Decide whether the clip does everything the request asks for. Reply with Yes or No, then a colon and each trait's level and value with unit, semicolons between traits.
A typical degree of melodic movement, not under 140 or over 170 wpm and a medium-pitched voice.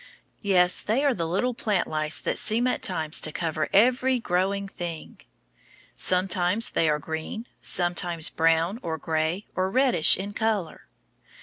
Yes: average, 4.9 semitones; average, 145 wpm; medium, 180 Hz